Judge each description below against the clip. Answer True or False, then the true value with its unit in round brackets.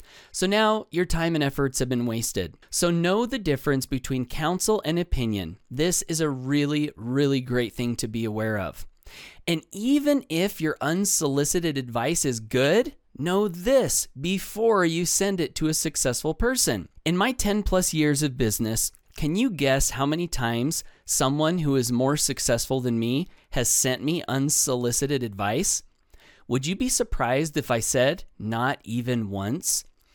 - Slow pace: False (160 wpm)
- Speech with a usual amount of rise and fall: False (5.9 semitones)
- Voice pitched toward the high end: False (145 Hz)